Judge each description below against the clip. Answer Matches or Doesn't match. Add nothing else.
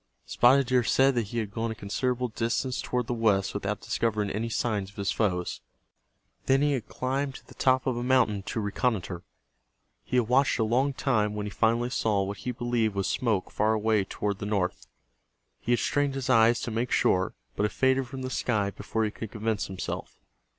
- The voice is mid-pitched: Doesn't match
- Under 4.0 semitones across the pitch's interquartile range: Matches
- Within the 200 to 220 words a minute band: Matches